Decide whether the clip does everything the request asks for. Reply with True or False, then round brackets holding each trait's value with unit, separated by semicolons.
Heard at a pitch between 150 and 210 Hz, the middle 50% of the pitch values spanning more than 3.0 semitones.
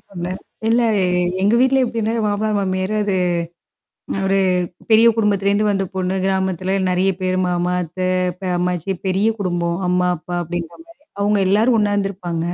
False (190 Hz; 2.5 semitones)